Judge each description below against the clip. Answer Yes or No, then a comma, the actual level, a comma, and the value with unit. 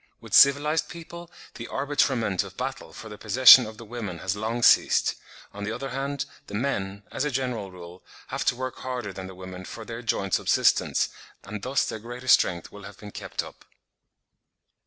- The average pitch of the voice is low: Yes, low, 115 Hz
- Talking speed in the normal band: Yes, average, 190 wpm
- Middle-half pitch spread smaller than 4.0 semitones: No, average, 4.5 semitones